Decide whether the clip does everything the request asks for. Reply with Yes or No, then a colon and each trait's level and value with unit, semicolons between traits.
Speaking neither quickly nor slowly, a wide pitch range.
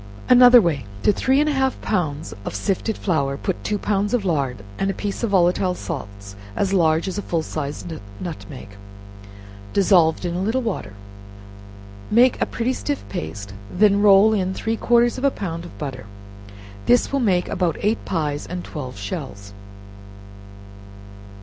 Yes: average, 160 wpm; wide, 5.7 semitones